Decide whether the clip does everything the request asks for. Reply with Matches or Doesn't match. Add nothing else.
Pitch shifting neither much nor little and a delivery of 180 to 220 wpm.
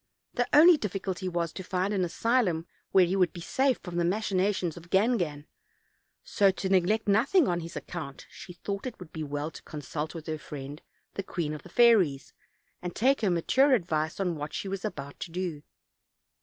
Matches